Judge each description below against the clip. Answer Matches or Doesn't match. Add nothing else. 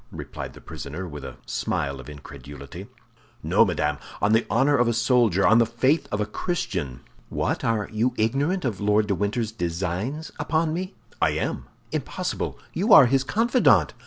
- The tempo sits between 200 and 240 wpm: Doesn't match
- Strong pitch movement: Matches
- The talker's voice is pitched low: Matches